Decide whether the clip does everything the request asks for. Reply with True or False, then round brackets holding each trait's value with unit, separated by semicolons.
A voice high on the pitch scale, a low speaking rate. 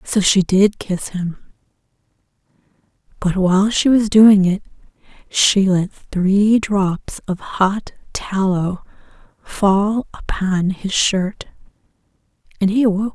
True (195 Hz; 115 wpm)